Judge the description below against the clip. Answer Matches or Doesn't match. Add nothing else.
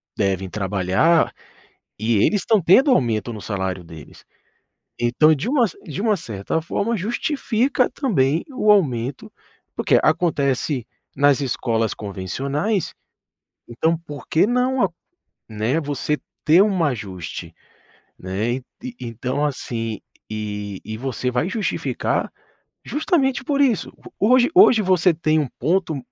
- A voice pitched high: Doesn't match